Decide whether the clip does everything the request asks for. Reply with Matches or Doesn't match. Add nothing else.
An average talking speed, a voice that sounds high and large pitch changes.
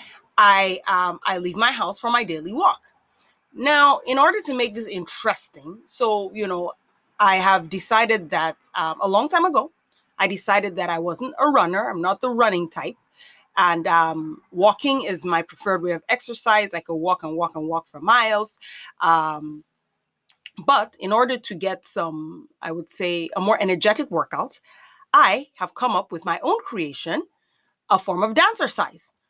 Matches